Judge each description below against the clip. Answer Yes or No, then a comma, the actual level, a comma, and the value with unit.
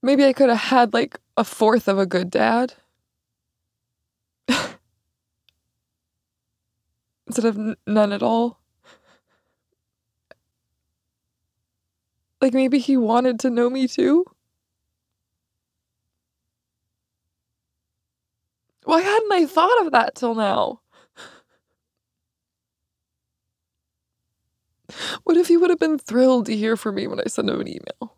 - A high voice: Yes, high, 220 Hz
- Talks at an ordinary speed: No, slow, 110 wpm